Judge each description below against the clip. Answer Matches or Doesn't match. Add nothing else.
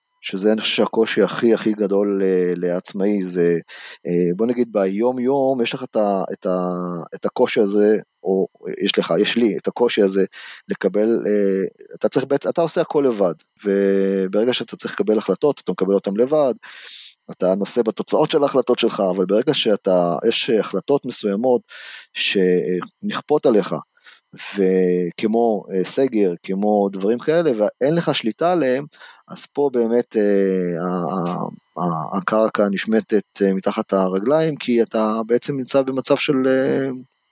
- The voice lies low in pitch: Matches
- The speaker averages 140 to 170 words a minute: Matches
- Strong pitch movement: Doesn't match